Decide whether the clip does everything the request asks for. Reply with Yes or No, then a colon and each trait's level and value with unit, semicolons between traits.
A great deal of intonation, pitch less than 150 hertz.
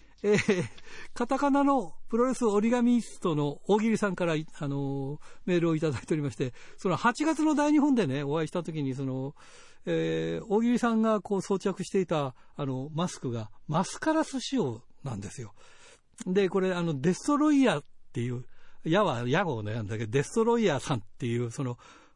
No: wide, 8.4 semitones; medium, 180 Hz